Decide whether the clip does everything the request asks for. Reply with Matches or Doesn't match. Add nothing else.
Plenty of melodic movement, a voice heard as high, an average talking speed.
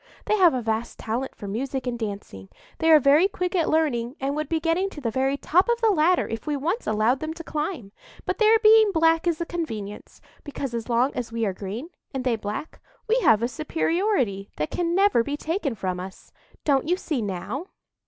Doesn't match